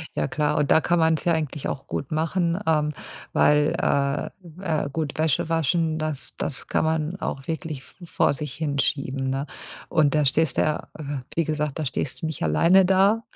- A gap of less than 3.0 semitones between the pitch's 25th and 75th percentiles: Yes, narrow, 2.4 semitones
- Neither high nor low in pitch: Yes, medium, 155 Hz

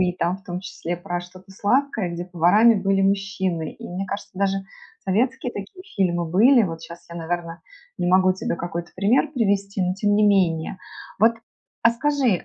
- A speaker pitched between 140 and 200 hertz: Yes, high, 190 Hz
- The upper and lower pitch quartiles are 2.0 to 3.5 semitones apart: Yes, average, 2.7 semitones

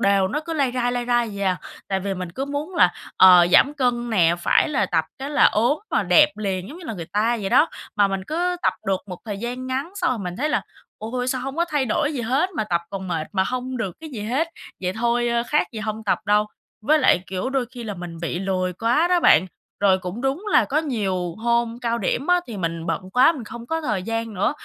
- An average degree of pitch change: No, wide, 6.0 semitones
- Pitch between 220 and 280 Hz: Yes, high, 235 Hz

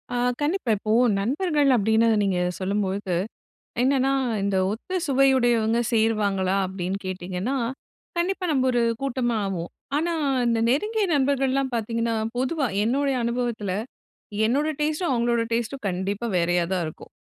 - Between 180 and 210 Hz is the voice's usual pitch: No, high, 235 Hz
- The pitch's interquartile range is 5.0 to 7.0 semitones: Yes, average, 5.3 semitones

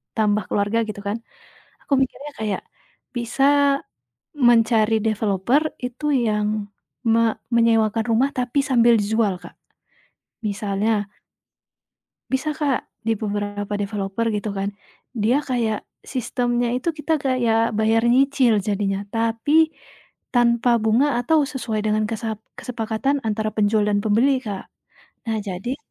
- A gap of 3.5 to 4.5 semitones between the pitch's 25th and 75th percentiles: No, average, 2.8 semitones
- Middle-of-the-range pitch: No, high, 225 Hz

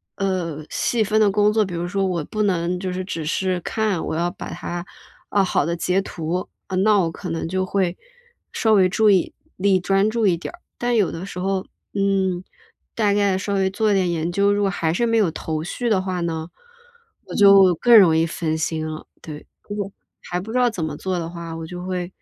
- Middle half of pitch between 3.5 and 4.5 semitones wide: No, average, 2.9 semitones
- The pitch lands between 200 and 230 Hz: No, medium, 185 Hz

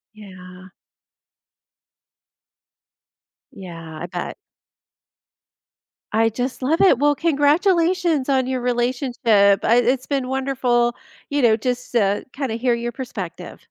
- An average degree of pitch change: Yes, average, 3.5 semitones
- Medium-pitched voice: No, very high, 250 Hz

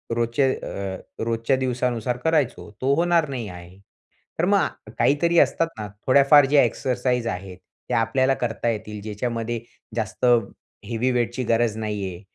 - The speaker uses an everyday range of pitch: Yes, average, 3.3 semitones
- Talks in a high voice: No, low, 120 Hz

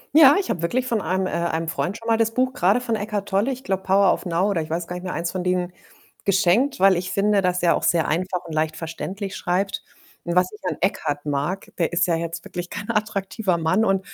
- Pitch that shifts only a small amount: No, average, 3.2 semitones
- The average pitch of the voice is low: No, medium, 185 Hz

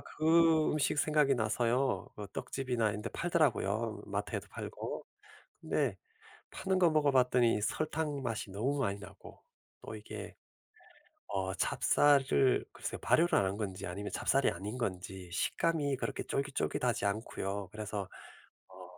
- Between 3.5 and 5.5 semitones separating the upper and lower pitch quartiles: No, wide, 6.2 semitones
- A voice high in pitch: No, low, 125 Hz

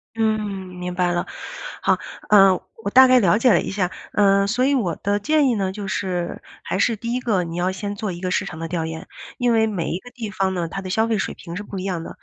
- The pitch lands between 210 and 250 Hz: No, high, 195 Hz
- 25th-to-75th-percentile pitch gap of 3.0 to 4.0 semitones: Yes, average, 3.6 semitones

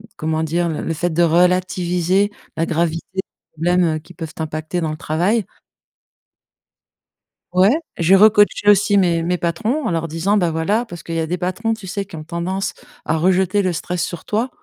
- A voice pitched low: No, medium, 175 Hz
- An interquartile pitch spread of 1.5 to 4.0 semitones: Yes, average, 3.0 semitones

